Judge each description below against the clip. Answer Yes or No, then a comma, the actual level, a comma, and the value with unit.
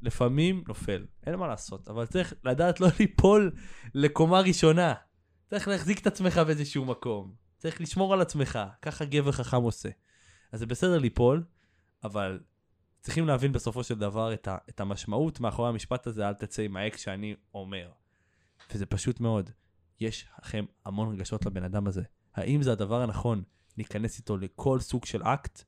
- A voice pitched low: Yes, low, 115 Hz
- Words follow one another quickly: Yes, fast, 160 wpm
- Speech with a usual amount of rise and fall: No, wide, 6.3 semitones